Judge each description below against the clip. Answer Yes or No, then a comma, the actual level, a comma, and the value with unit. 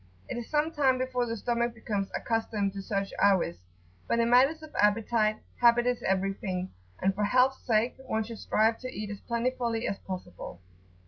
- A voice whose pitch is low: No, high, 230 Hz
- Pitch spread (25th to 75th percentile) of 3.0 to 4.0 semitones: Yes, average, 3.5 semitones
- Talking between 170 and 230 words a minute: Yes, average, 180 wpm